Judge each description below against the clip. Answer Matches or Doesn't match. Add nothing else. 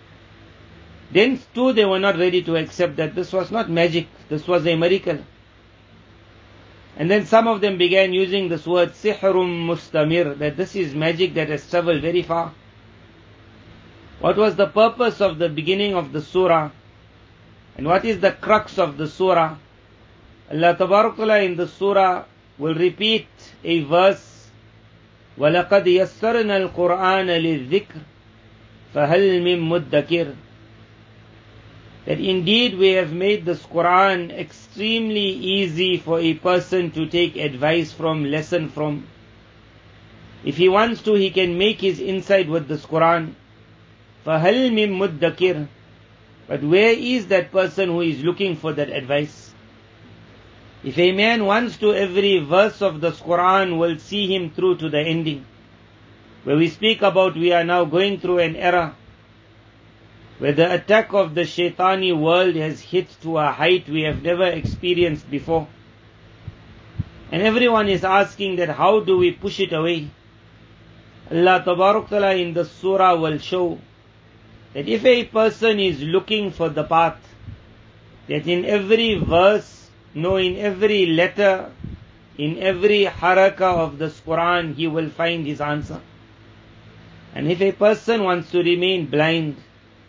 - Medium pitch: Matches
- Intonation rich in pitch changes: Matches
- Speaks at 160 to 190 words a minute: Doesn't match